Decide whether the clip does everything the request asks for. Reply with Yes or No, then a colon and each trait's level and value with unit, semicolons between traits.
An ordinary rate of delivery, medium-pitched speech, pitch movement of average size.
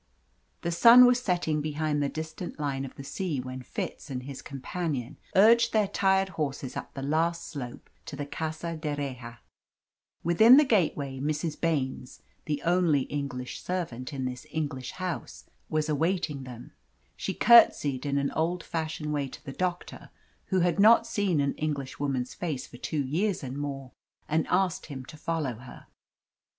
Yes: average, 160 wpm; medium, 150 Hz; average, 4.3 semitones